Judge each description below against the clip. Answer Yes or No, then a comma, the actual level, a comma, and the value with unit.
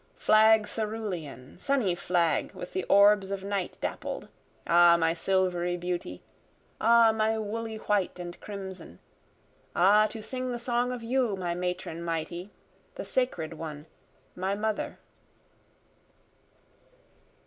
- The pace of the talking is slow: Yes, slow, 120 wpm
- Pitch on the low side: No, high, 195 Hz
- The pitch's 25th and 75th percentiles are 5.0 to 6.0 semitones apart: No, average, 4.1 semitones